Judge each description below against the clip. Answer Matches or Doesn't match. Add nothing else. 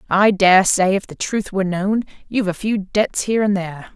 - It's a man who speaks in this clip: Doesn't match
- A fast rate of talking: Matches